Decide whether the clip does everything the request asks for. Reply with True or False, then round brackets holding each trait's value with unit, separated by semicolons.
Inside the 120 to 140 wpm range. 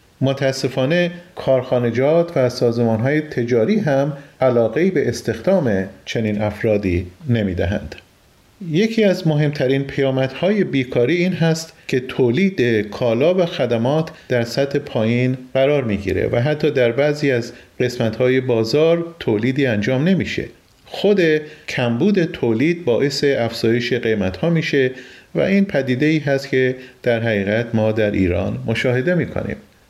True (135 wpm)